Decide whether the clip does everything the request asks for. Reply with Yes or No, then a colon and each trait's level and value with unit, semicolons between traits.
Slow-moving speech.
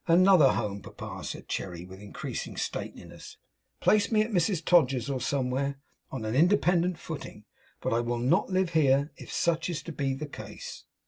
No: average, 175 wpm